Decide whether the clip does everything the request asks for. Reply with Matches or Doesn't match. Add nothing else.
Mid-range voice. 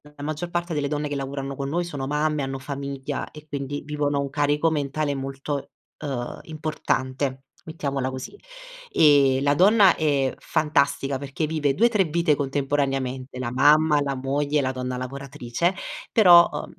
Matches